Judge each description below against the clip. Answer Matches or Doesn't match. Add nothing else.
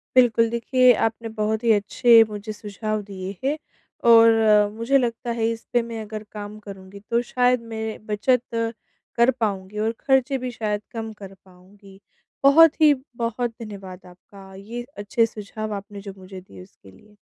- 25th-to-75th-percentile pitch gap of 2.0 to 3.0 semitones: Matches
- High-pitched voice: Matches